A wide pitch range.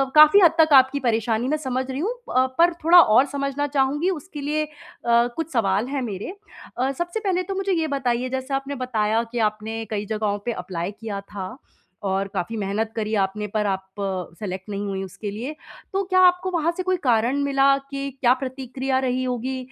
Yes: wide, 5.8 semitones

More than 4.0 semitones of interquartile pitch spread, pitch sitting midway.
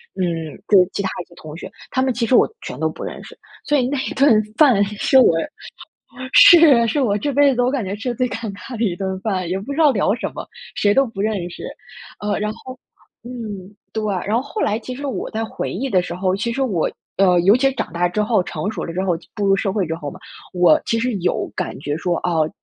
No: average, 5.2 semitones; high, 210 Hz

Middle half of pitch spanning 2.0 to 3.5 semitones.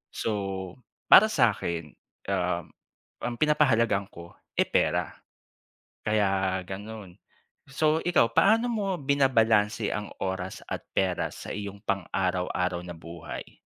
No: average, 4.5 semitones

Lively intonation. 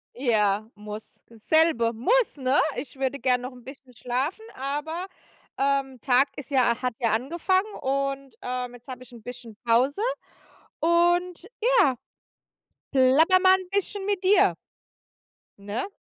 Yes: wide, 5.7 semitones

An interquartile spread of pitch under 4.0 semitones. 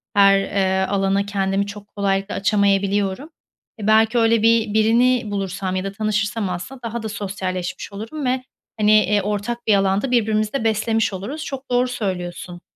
Yes: narrow, 2.5 semitones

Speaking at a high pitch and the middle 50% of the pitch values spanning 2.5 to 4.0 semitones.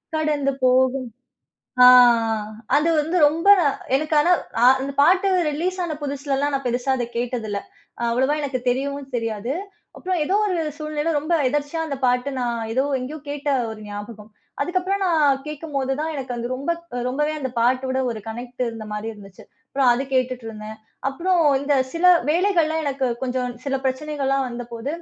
Yes: very high, 275 Hz; average, 3.6 semitones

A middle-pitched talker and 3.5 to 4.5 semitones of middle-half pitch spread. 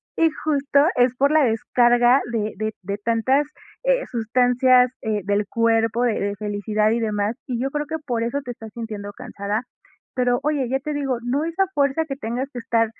No: high, 245 Hz; average, 3.8 semitones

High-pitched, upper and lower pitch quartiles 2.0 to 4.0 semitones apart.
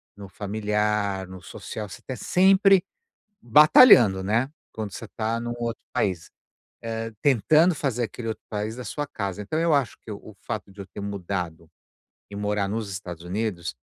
No: low, 105 Hz; average, 3.3 semitones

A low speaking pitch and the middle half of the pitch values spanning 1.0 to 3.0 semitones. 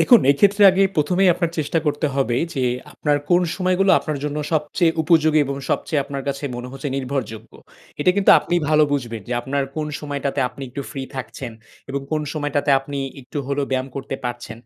No: medium, 145 Hz; average, 2.7 semitones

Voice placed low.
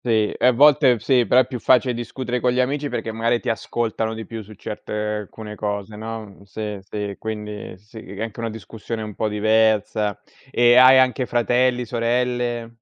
Yes: low, 115 Hz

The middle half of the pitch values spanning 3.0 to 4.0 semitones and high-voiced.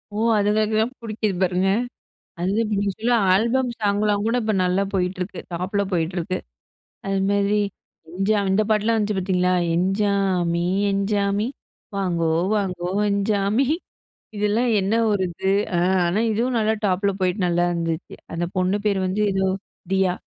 No: narrow, 2.5 semitones; high, 200 Hz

